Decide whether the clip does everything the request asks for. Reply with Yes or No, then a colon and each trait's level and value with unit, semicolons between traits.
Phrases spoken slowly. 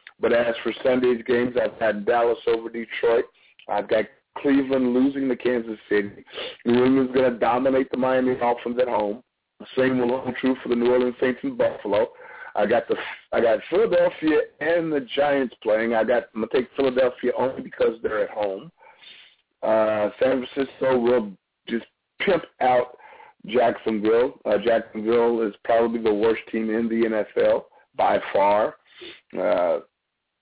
No: average, 155 wpm